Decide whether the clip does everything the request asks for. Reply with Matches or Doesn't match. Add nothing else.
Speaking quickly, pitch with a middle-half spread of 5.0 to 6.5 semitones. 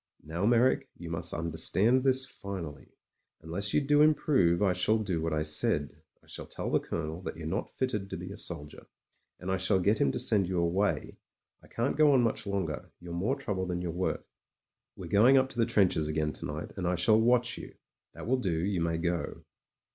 Matches